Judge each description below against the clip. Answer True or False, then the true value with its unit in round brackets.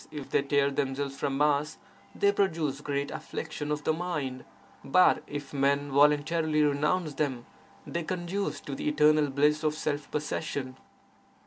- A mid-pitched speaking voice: True (150 Hz)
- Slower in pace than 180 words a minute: True (145 wpm)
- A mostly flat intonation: True (1.6 semitones)